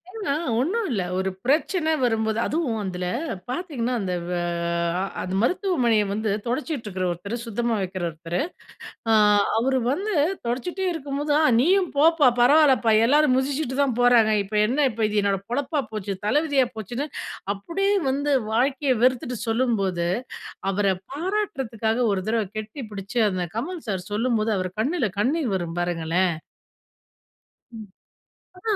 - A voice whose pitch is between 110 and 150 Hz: No, high, 240 Hz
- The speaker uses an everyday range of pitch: No, wide, 5.8 semitones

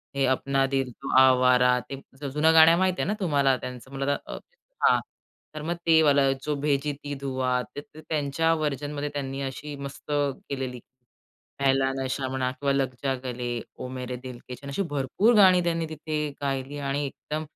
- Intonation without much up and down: Yes, narrow, 2.2 semitones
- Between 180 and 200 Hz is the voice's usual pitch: No, medium, 140 Hz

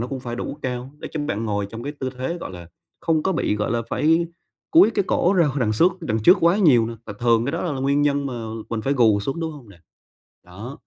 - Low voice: Yes, low, 130 Hz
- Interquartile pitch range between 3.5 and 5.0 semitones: No, wide, 5.4 semitones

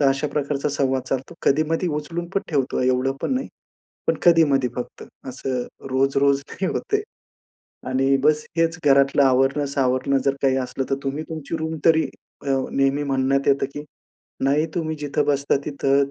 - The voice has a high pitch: No, medium, 140 Hz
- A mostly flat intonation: Yes, narrow, 2.2 semitones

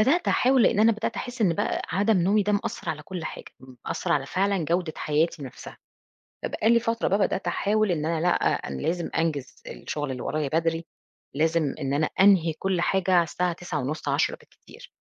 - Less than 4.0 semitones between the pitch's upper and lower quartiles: No, average, 4.6 semitones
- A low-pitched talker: No, medium, 175 Hz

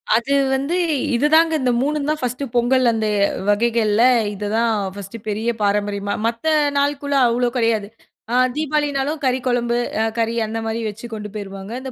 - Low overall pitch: No, high, 235 Hz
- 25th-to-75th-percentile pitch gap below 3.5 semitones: No, average, 4.3 semitones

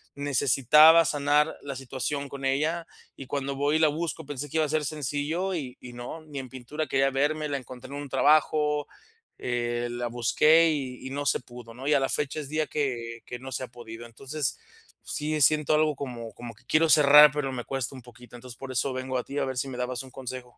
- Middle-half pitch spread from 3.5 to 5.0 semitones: No, average, 3.0 semitones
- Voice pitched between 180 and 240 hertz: No, low, 135 Hz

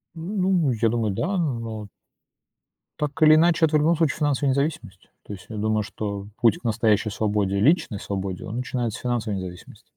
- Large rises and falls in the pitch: Yes, wide, 6.5 semitones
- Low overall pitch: Yes, low, 115 Hz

